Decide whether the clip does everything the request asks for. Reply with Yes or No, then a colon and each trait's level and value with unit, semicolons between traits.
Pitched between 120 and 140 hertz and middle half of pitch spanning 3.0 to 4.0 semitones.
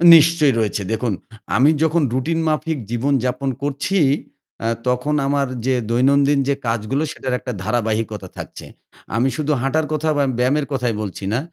Yes: low, 135 Hz; average, 3.7 semitones